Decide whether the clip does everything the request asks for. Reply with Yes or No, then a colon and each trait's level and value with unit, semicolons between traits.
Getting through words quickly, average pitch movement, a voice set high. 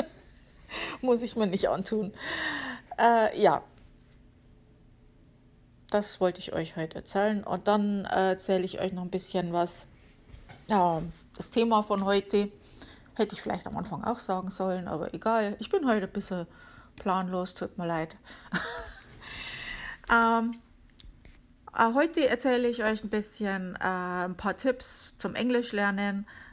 No: average, 140 wpm; average, 3.4 semitones; high, 200 Hz